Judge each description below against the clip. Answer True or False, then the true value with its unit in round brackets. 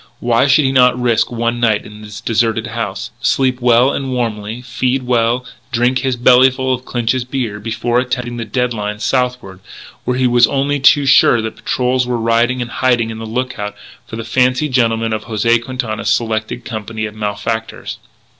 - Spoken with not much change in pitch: True (2.1 semitones)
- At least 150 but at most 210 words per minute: True (180 wpm)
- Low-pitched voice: True (120 Hz)